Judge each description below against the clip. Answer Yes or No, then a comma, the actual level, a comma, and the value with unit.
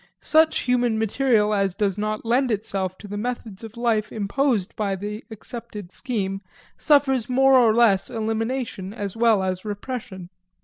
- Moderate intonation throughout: Yes, average, 3.4 semitones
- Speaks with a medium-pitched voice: No, high, 220 Hz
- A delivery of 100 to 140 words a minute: No, average, 150 wpm